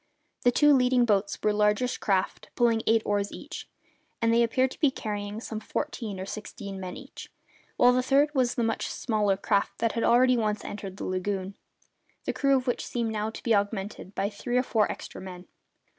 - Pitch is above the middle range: Yes, high, 220 Hz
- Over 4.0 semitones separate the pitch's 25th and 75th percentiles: No, average, 3.4 semitones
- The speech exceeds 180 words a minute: Yes, average, 200 wpm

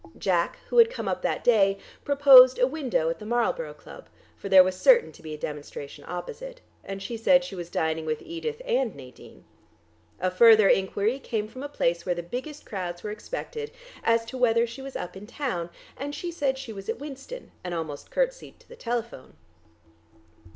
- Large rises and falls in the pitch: Yes, wide, 7.5 semitones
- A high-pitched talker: Yes, high, 230 Hz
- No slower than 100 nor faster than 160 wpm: No, average, 195 wpm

